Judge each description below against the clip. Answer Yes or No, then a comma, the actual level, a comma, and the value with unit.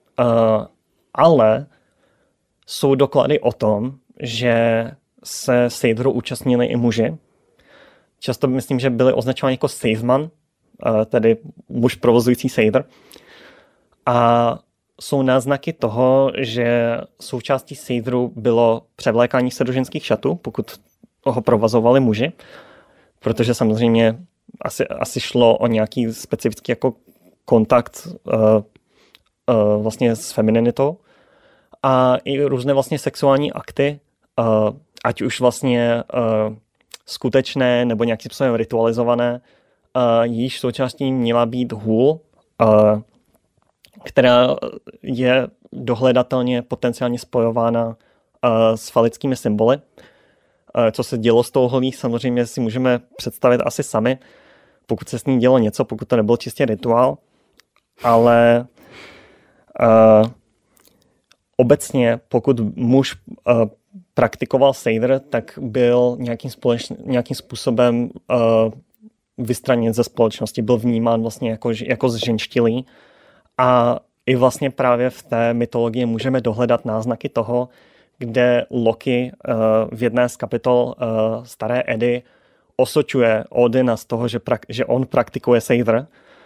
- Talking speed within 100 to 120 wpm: Yes, slow, 115 wpm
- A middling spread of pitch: No, narrow, 2.1 semitones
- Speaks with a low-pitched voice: Yes, low, 120 Hz